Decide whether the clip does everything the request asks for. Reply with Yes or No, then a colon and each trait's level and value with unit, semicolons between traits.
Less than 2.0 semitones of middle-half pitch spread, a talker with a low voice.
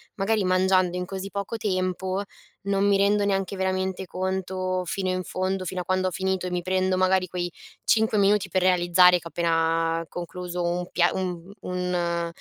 No: narrow, 1.2 semitones; medium, 185 Hz